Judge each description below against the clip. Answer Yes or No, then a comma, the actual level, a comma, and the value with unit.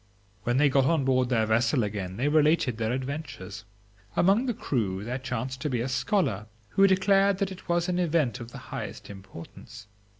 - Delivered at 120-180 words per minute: No, average, 190 wpm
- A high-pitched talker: No, low, 130 Hz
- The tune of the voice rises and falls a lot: Yes, wide, 6.8 semitones